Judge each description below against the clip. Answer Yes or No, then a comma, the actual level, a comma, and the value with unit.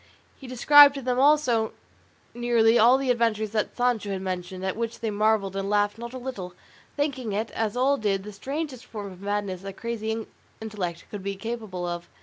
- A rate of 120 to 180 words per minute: No, average, 190 wpm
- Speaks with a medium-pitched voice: No, high, 220 Hz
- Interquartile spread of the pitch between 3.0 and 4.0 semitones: Yes, average, 3.7 semitones